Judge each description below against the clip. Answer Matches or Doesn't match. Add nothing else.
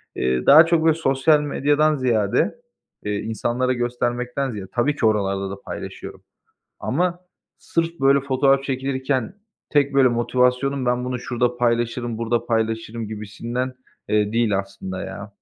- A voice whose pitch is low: Matches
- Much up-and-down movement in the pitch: Doesn't match